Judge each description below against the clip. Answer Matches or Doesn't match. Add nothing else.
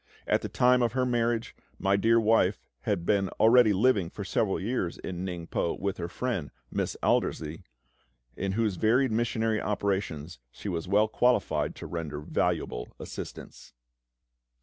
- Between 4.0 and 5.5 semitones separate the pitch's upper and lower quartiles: Matches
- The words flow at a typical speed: Matches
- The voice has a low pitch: Matches